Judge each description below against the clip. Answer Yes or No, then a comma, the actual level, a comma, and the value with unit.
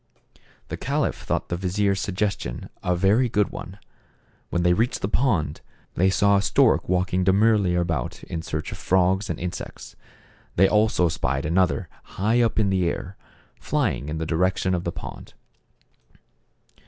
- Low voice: Yes, very low, 95 Hz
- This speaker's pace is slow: No, average, 160 wpm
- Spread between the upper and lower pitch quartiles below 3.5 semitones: Yes, narrow, 2.6 semitones